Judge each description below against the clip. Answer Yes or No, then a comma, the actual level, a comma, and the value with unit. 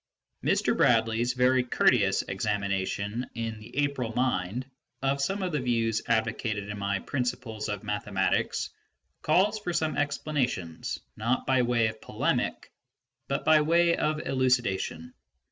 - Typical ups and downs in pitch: Yes, average, 4.8 semitones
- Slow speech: Yes, slow, 130 wpm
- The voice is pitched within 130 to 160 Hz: No, low, 120 Hz